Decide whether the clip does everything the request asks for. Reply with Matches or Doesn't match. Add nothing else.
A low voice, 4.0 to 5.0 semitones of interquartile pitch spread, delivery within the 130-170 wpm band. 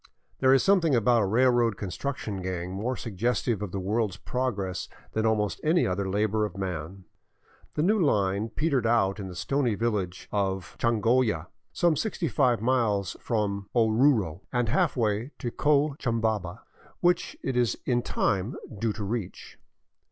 Matches